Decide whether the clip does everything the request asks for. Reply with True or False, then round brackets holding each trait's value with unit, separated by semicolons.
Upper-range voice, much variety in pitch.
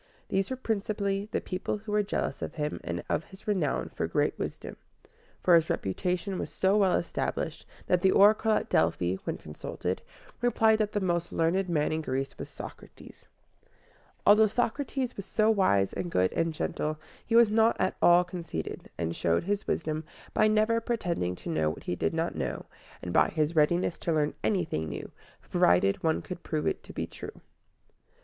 False (180 Hz; 5.7 semitones)